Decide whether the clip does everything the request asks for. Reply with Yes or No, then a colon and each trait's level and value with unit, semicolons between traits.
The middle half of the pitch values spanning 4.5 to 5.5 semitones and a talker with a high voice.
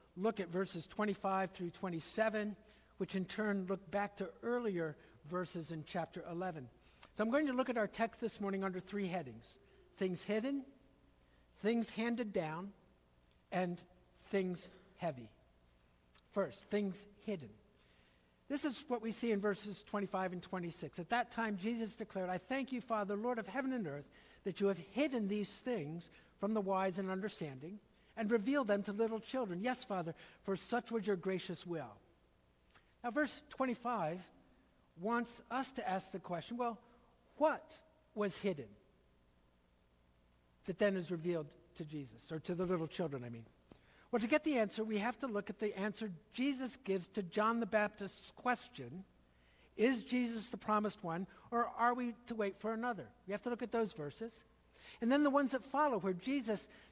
Yes: average, 4.8 semitones; high, 200 Hz